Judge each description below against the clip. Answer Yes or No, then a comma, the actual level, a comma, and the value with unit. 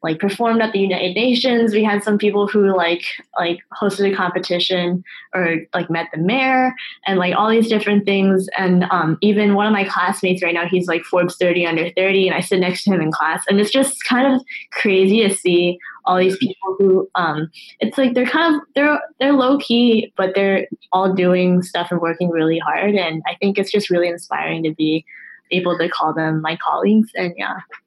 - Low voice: No, high, 190 Hz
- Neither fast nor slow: No, fast, 210 wpm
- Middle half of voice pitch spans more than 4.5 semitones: No, average, 3.2 semitones